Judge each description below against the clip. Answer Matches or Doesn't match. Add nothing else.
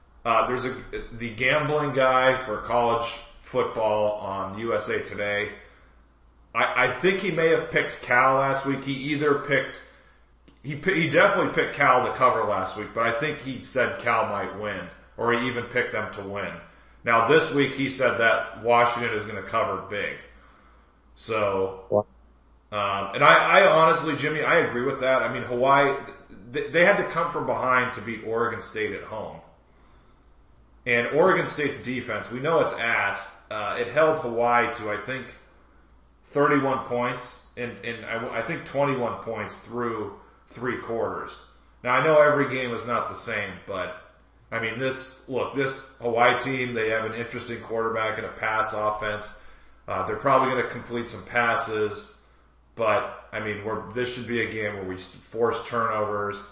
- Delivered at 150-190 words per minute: Matches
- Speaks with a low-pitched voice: Matches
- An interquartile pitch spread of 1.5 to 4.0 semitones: Matches